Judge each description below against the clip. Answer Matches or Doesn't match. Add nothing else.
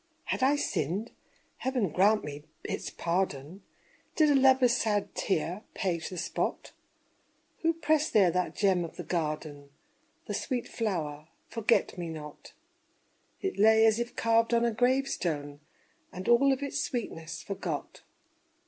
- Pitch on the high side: Matches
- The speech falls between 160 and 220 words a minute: Doesn't match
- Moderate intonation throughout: Doesn't match